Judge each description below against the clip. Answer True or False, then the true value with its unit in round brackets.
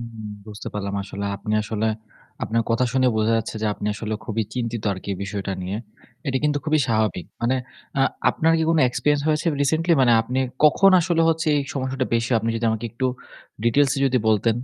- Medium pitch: False (115 Hz)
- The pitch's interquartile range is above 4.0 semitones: True (4.6 semitones)